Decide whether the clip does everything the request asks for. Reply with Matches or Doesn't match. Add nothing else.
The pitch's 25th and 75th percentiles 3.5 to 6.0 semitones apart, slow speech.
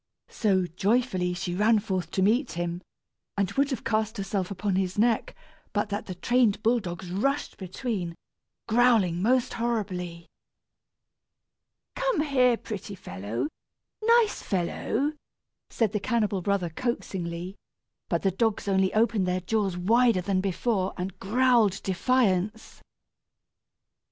Matches